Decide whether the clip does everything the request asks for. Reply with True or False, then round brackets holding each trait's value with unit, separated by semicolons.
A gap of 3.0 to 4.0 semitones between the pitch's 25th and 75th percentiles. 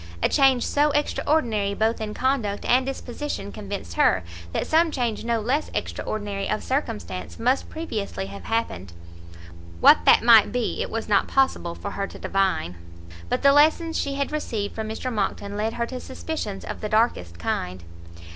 False (5.1 semitones)